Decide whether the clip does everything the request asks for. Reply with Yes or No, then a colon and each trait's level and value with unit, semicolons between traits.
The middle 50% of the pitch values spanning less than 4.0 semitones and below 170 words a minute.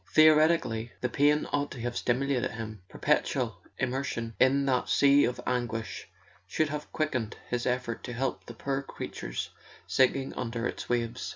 Yes: average, 2.9 semitones; average, 160 wpm